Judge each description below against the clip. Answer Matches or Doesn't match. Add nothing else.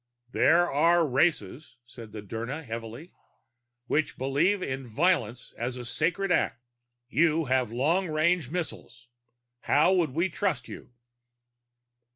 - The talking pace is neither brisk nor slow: Doesn't match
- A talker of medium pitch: Matches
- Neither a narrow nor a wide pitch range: Doesn't match